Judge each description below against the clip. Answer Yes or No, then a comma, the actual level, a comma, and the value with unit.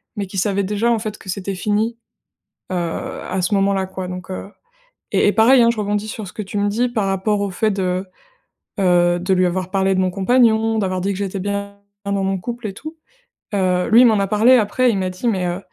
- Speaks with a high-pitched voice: Yes, high, 200 Hz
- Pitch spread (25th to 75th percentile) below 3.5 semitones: Yes, narrow, 2.6 semitones